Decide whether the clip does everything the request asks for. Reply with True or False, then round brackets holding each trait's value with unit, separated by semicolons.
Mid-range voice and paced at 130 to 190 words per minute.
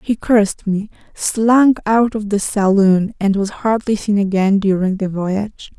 False (205 Hz; 165 wpm)